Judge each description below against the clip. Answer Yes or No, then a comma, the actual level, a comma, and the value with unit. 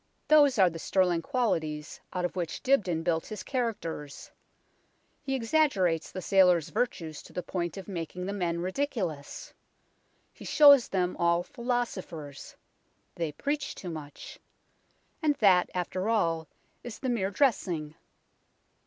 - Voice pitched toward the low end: No, medium, 185 Hz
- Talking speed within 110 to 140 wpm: Yes, slow, 135 wpm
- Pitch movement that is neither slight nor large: No, wide, 6.2 semitones